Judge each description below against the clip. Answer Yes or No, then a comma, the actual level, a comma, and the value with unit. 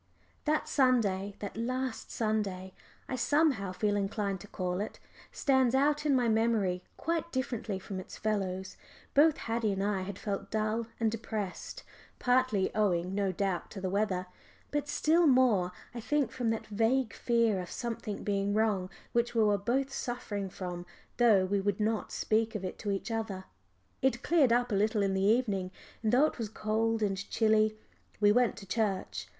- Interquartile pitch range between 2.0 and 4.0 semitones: Yes, average, 3.6 semitones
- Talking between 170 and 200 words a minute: Yes, average, 175 wpm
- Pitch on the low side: No, high, 215 Hz